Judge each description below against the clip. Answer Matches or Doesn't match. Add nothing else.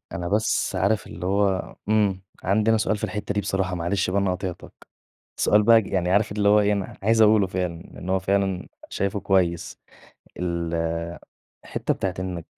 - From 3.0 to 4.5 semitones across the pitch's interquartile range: Doesn't match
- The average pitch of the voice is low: Matches